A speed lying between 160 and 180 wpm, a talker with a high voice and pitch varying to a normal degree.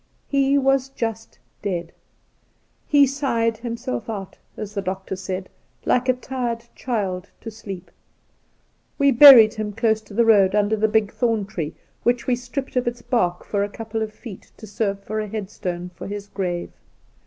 Yes: average, 170 wpm; high, 220 Hz; average, 3.4 semitones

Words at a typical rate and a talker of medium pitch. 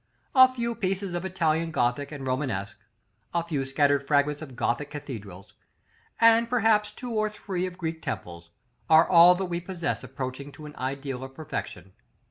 Yes: average, 165 wpm; medium, 155 Hz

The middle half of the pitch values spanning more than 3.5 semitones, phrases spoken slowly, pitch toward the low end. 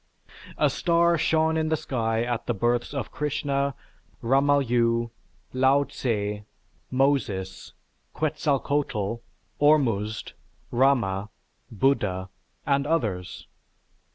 Yes: average, 4.3 semitones; slow, 95 wpm; low, 130 Hz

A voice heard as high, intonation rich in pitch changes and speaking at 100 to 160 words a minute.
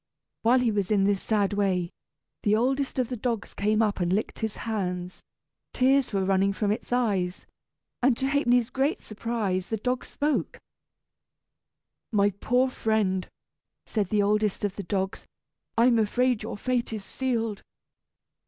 No: high, 215 Hz; average, 3.8 semitones; average, 155 wpm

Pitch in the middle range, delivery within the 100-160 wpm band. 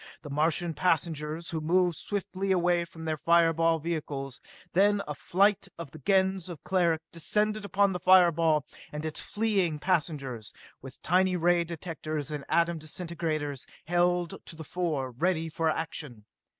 Yes: medium, 165 Hz; average, 150 wpm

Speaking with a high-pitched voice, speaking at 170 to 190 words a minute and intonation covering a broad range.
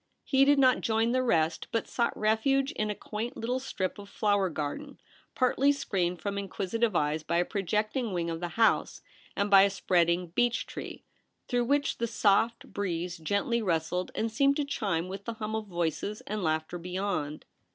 No: high, 205 Hz; average, 185 wpm; average, 4.9 semitones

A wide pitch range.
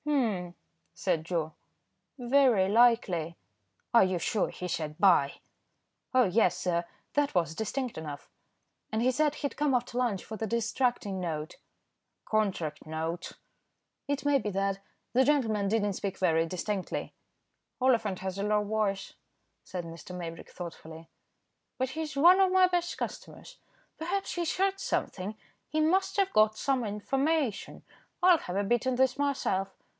Yes: wide, 6.9 semitones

